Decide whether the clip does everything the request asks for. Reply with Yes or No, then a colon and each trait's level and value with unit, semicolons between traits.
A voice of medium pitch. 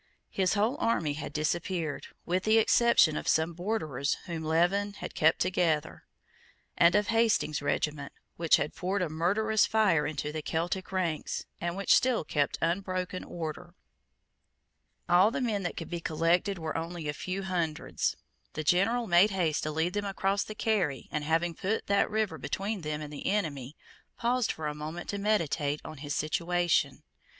Yes: medium, 175 Hz